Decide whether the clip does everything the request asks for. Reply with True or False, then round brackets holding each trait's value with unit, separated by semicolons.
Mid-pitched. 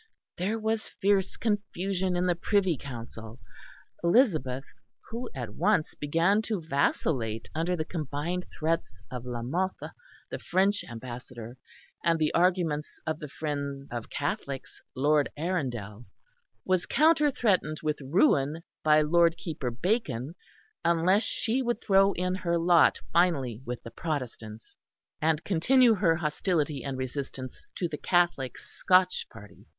True (160 Hz)